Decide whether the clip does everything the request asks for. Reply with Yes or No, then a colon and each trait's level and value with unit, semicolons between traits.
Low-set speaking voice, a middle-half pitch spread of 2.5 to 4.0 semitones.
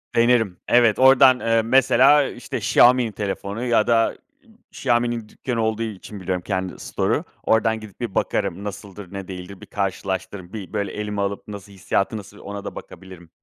Yes: low, 105 Hz; average, 3.1 semitones